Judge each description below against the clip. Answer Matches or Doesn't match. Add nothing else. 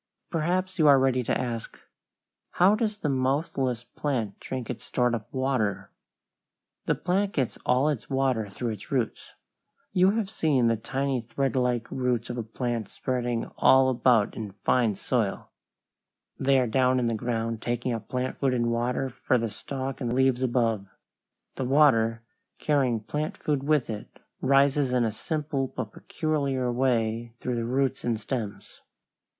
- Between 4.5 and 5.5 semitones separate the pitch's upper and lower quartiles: Doesn't match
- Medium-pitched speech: Doesn't match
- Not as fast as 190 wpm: Matches